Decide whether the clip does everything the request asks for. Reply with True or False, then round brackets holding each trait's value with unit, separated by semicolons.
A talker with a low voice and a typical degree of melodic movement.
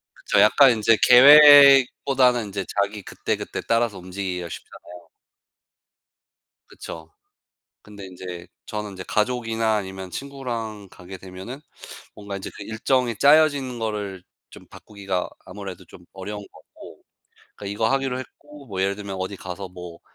True (105 Hz; 4.5 semitones)